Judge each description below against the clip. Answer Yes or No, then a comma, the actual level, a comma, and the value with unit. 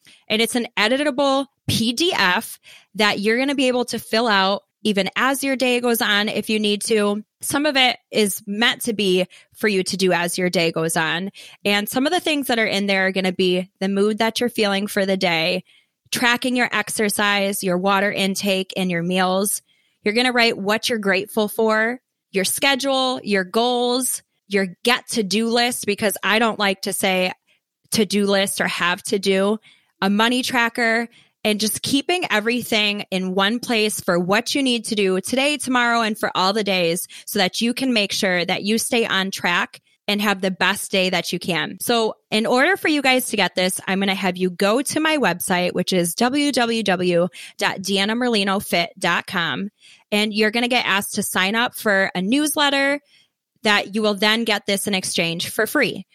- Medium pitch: No, high, 210 Hz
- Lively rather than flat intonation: No, average, 3.8 semitones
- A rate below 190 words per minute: No, average, 195 wpm